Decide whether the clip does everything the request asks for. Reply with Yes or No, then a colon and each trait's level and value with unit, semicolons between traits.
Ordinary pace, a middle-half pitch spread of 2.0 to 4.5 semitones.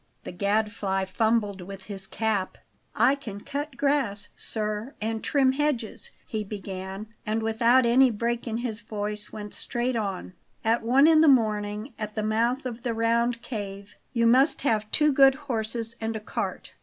Yes: average, 170 wpm; average, 2.9 semitones